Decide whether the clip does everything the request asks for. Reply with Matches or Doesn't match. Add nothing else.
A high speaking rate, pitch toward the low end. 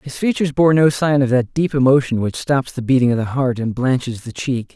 Matches